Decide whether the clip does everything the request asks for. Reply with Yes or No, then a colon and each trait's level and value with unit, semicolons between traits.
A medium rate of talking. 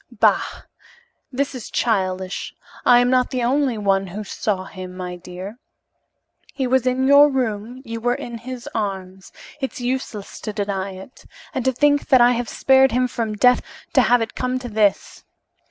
Yes: average, 175 wpm